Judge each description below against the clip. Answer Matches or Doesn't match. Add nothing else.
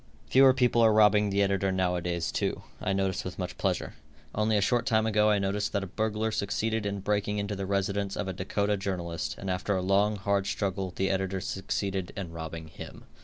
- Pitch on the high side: Doesn't match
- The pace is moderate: Doesn't match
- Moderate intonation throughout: Doesn't match